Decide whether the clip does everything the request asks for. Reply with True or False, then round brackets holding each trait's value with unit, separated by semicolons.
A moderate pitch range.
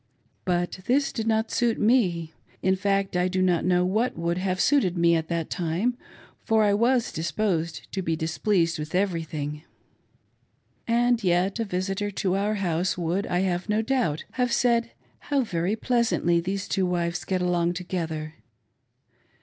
True (4.2 semitones)